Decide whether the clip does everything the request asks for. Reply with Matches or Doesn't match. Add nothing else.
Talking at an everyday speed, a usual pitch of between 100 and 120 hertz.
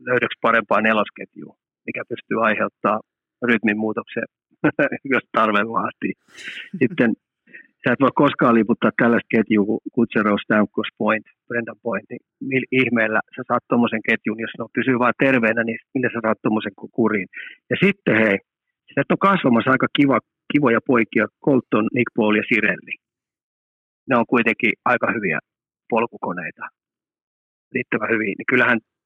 Matches